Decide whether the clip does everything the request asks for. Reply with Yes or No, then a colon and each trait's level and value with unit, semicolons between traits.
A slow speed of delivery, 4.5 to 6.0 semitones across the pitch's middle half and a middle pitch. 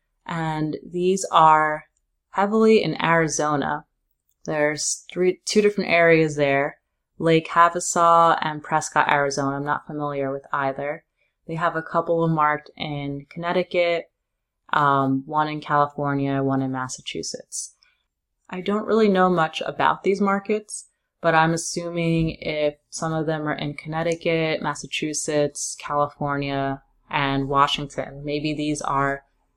No: slow, 125 wpm; average, 2.7 semitones; medium, 155 Hz